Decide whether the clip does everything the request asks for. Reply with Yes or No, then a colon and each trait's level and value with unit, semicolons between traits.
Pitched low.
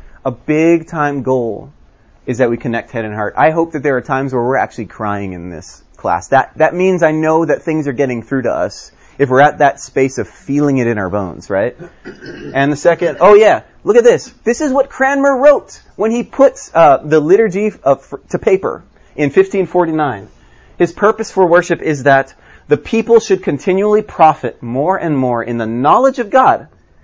No: medium, 150 Hz